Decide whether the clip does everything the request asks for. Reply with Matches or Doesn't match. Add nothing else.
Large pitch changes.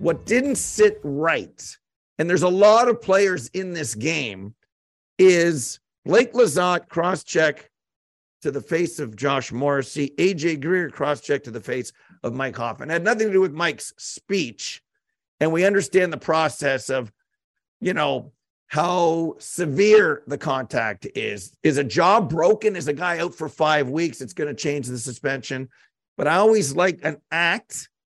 Doesn't match